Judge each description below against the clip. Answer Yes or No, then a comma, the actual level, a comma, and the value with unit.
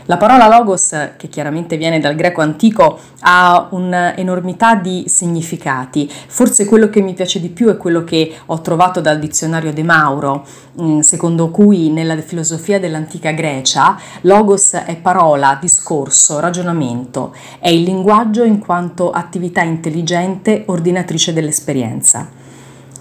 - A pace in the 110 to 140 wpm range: Yes, average, 130 wpm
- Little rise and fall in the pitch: No, average, 3.0 semitones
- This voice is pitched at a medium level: Yes, medium, 170 Hz